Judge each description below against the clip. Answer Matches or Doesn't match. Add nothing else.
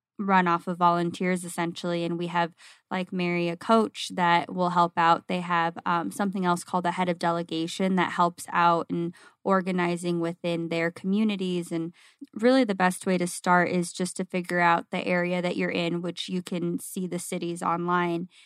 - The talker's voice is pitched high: Doesn't match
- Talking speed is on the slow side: Doesn't match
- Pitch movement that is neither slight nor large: Doesn't match